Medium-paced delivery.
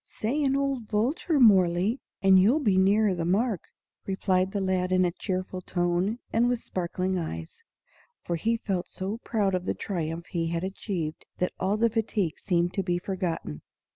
Yes: average, 170 wpm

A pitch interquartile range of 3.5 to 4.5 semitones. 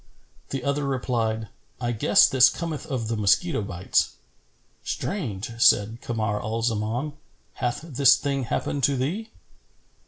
Yes: average, 4.1 semitones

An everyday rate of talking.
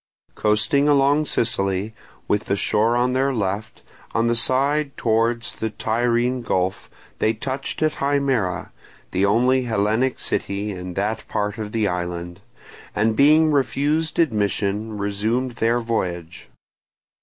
No: slow, 130 wpm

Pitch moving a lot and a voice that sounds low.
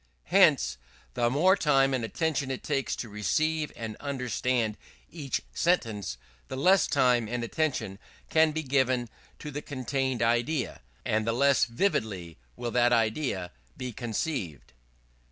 No: average, 4.3 semitones; low, 125 Hz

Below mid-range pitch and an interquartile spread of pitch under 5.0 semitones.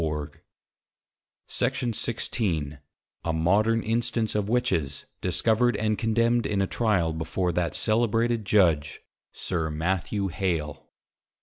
No: low, 100 Hz; wide, 5.6 semitones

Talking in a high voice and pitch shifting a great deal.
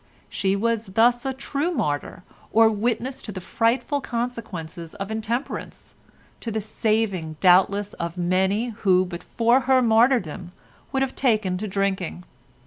No: high, 215 Hz; average, 4.3 semitones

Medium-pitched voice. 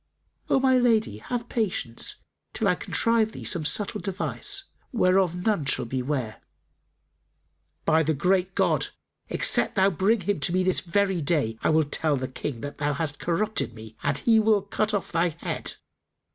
Yes: medium, 180 Hz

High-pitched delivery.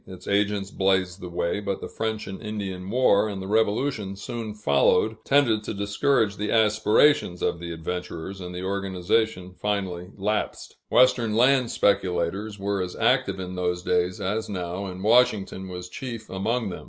No: low, 100 Hz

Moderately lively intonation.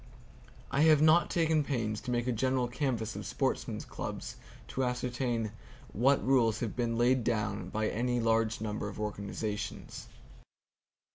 Yes: average, 3.1 semitones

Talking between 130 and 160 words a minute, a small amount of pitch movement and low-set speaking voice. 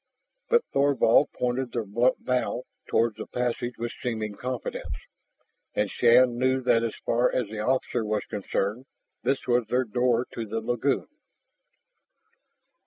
Yes: average, 140 wpm; narrow, 2.1 semitones; low, 120 Hz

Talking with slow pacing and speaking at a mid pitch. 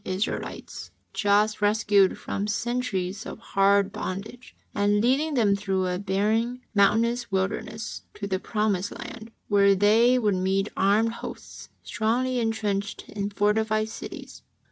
No: slow, 125 wpm; high, 210 Hz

